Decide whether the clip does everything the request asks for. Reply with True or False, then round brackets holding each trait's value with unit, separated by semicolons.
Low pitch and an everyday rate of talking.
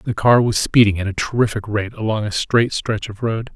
False (110 Hz; 235 wpm)